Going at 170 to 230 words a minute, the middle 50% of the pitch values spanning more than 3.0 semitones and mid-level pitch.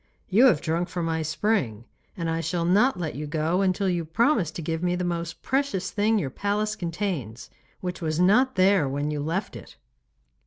Yes: average, 195 wpm; average, 4.1 semitones; medium, 175 Hz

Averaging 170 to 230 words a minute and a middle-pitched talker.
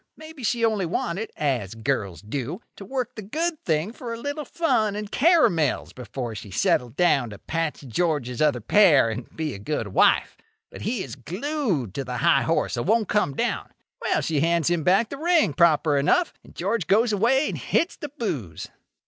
Yes: average, 190 wpm; medium, 170 Hz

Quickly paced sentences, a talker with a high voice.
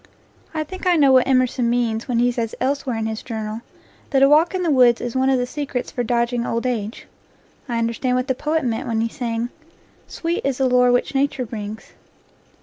Yes: fast, 215 wpm; very high, 250 Hz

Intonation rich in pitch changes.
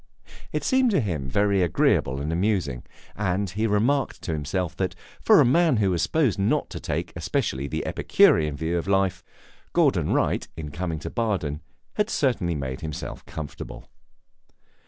Yes: wide, 5.7 semitones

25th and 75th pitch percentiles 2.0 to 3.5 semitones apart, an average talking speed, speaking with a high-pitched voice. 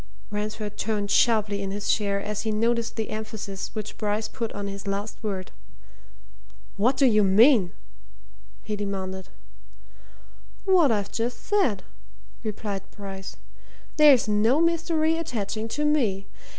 No: average, 2.9 semitones; slow, 130 wpm; high, 215 Hz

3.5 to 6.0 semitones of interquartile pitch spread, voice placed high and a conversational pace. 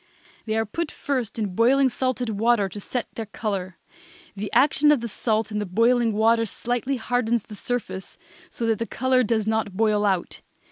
No: average, 2.8 semitones; high, 225 Hz; average, 185 wpm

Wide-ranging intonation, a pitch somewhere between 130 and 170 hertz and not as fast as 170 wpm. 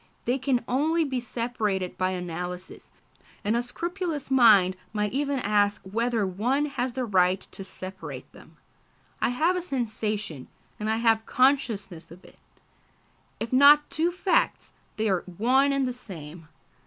No: wide, 5.8 semitones; high, 230 Hz; average, 150 wpm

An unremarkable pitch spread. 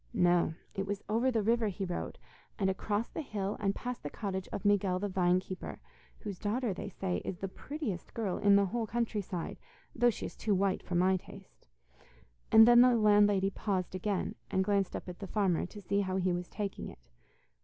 No: narrow, 2.3 semitones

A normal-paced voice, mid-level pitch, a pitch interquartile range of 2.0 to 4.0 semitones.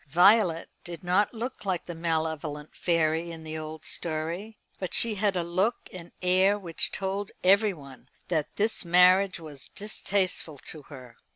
Yes: average, 155 wpm; medium, 175 Hz; average, 3.7 semitones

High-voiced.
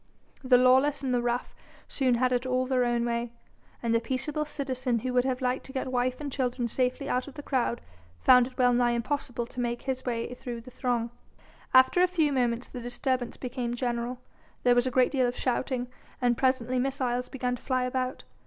Yes: very high, 250 Hz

